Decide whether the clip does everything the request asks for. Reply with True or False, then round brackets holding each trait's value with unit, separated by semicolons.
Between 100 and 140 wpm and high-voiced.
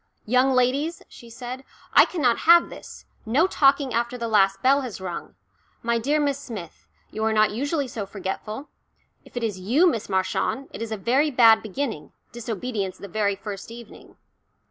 False (175 wpm; 235 Hz)